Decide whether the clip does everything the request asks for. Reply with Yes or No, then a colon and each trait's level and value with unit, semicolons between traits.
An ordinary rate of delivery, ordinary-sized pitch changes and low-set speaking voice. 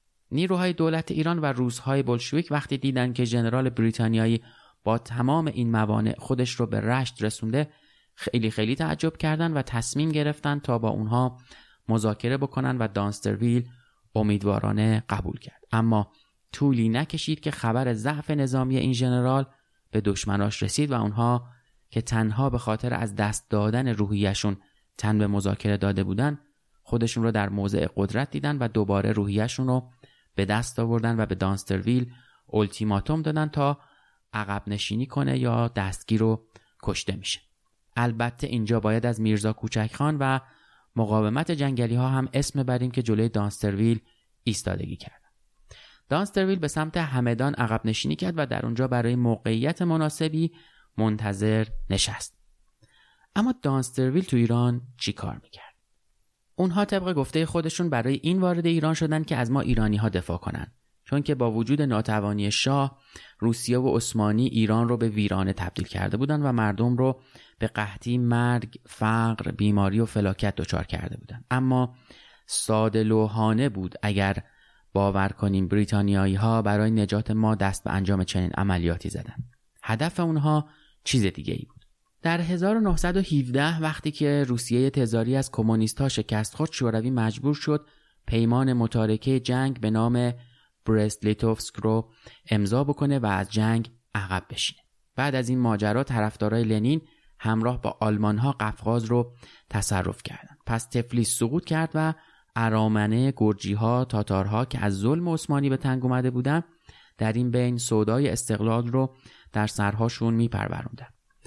Yes: average, 145 wpm; average, 4.0 semitones; low, 120 Hz